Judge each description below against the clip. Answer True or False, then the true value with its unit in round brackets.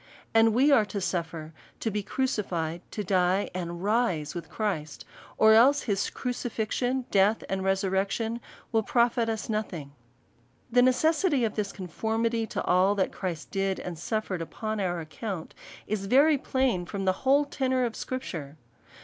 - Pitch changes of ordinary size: True (4.5 semitones)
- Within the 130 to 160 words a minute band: True (155 wpm)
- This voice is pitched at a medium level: False (210 Hz)